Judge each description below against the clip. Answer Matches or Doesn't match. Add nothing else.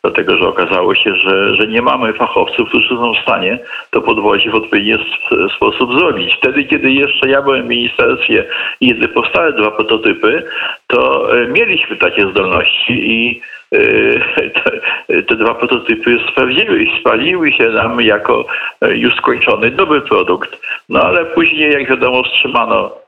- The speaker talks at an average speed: Matches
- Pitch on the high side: Matches